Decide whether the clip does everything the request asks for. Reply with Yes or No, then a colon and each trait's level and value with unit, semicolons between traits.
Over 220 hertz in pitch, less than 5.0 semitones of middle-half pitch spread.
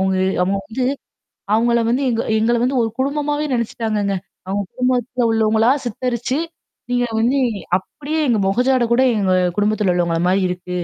Yes: high, 230 Hz; average, 3.8 semitones